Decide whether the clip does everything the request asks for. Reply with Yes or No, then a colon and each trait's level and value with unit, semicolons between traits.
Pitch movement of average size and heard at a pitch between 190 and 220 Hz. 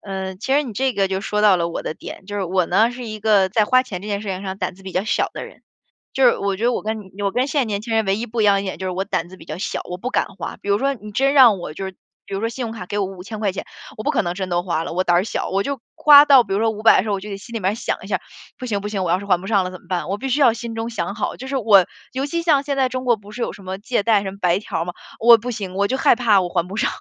Yes: average, 3.7 semitones; high, 205 Hz